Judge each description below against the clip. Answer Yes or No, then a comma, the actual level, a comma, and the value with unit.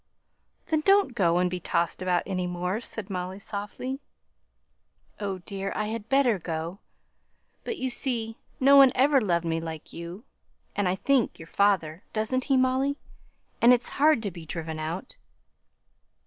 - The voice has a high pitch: Yes, high, 200 Hz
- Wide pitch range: Yes, wide, 6.6 semitones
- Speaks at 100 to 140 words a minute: No, average, 160 wpm